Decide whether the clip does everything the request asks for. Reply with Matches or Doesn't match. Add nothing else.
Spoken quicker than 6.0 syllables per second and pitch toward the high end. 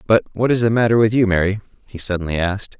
Doesn't match